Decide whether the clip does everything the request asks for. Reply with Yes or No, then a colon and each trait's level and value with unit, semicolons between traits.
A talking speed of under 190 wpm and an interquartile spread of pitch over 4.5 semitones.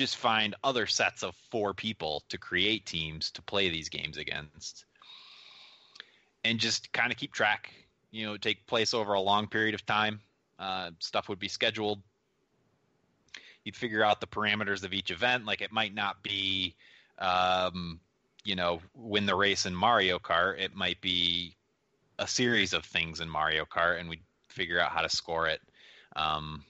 No: average, 175 wpm; average, 3.6 semitones